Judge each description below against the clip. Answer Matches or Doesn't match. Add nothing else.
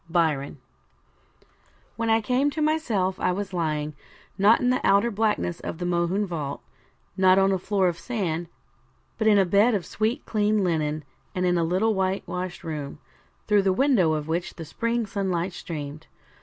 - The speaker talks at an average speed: Matches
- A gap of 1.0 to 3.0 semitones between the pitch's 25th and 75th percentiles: Doesn't match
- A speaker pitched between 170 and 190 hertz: Matches